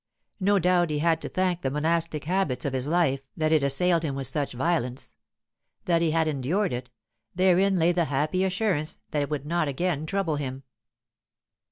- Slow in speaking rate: No, average, 185 wpm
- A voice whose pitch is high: No, medium, 160 Hz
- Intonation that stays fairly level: No, average, 3.9 semitones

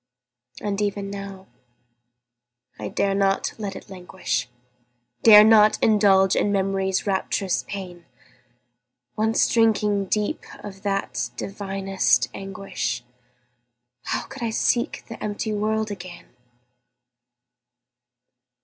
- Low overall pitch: No, high, 195 Hz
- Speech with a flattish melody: Yes, narrow, 1.6 semitones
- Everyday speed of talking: No, slow, 100 wpm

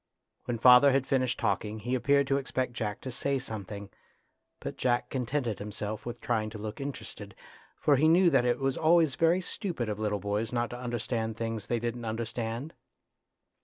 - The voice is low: Yes, low, 120 Hz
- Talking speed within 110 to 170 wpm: No, average, 180 wpm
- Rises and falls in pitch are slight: No, average, 3.7 semitones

